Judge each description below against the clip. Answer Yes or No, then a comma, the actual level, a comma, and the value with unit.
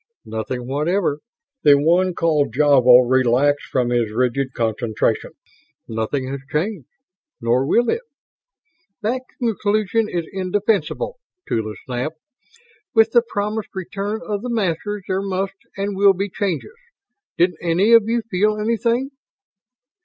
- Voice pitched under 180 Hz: No, medium, 185 Hz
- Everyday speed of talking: No, slow, 125 wpm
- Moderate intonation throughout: No, wide, 8.1 semitones